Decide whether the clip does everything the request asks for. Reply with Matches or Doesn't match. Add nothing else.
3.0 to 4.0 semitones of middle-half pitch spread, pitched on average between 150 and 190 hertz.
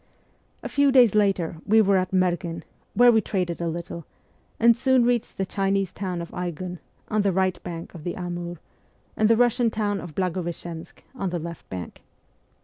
Matches